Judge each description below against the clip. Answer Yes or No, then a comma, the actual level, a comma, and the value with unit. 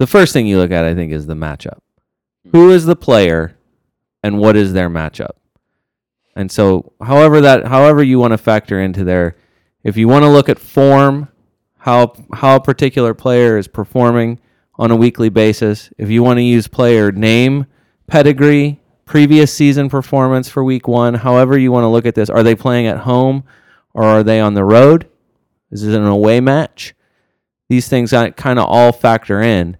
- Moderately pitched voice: No, low, 120 Hz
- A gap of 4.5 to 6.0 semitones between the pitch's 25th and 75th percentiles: No, average, 3.9 semitones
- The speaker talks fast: No, average, 185 wpm